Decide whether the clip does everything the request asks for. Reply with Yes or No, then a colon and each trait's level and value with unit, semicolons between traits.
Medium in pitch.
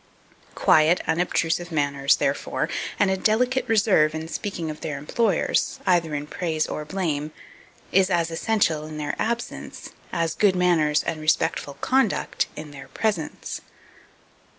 Yes: medium, 165 Hz